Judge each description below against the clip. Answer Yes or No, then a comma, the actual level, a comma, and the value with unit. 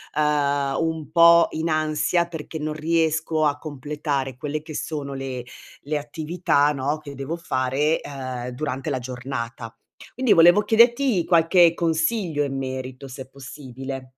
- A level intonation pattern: No, average, 3.4 semitones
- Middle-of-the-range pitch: Yes, medium, 150 Hz